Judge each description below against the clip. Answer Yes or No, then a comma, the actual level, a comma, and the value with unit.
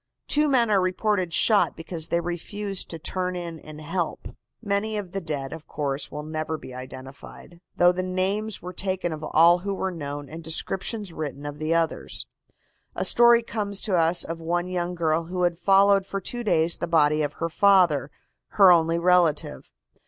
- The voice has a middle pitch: Yes, medium, 175 Hz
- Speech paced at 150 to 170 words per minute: No, average, 185 wpm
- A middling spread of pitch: Yes, average, 3.5 semitones